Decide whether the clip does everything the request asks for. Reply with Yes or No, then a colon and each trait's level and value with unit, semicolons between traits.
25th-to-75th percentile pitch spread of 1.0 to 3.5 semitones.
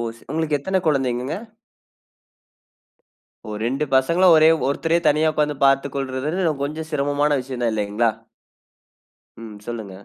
No: average, 3.9 semitones